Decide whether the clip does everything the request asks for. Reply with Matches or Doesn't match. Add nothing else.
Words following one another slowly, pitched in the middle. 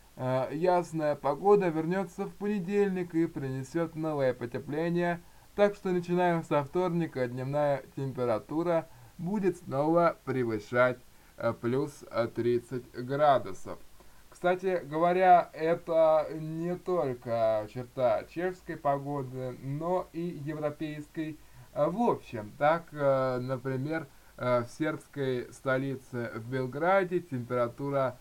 Matches